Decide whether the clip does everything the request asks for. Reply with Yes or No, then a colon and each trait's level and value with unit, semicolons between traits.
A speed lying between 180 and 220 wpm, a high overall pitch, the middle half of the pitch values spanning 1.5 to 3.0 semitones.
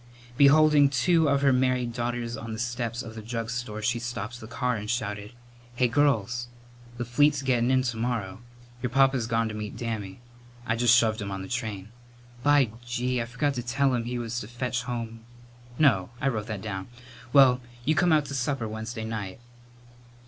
No: average, 190 wpm; low, 120 Hz; narrow, 2.5 semitones